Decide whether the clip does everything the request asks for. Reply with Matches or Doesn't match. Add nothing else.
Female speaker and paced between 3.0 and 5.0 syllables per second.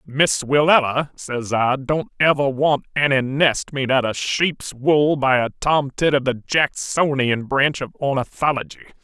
Doesn't match